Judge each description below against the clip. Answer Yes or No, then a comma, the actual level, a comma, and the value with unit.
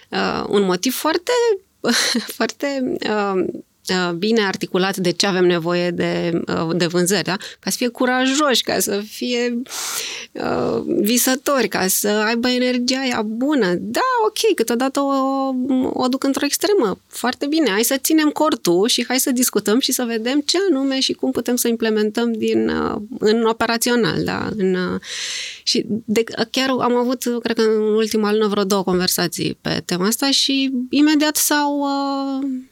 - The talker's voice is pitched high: Yes, high, 240 Hz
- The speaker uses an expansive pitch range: No, average, 4.7 semitones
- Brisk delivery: No, average, 155 wpm